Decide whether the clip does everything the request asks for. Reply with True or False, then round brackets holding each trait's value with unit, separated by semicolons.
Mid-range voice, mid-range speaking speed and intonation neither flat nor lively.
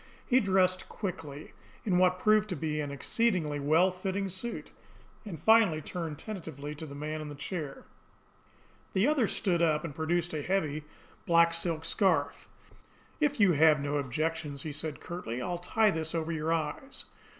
True (165 Hz; 165 wpm; 3.8 semitones)